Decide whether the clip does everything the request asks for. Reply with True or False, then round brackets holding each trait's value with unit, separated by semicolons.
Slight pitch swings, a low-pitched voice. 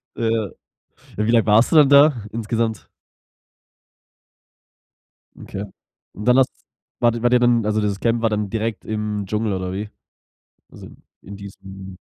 True (2.3 semitones; 110 Hz)